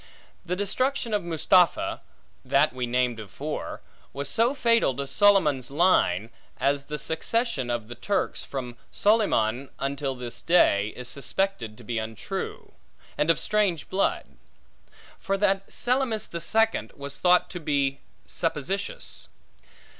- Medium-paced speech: No, slow, 130 wpm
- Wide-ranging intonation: Yes, wide, 7.6 semitones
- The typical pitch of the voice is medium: Yes, medium, 150 Hz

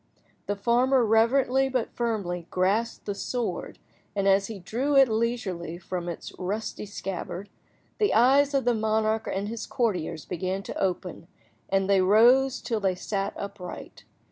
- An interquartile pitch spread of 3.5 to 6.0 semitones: Yes, average, 4.0 semitones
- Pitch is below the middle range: No, high, 210 Hz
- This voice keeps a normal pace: Yes, average, 150 wpm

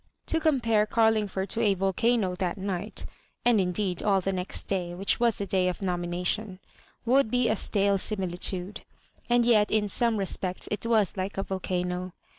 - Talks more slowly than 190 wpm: Yes, average, 170 wpm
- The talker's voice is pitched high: Yes, high, 195 Hz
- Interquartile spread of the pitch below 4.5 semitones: Yes, average, 3.2 semitones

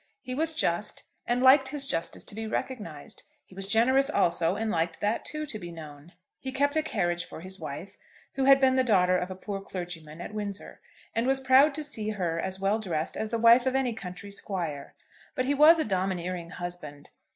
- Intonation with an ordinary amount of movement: No, wide, 6.8 semitones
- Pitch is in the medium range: No, high, 205 Hz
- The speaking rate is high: Yes, fast, 210 wpm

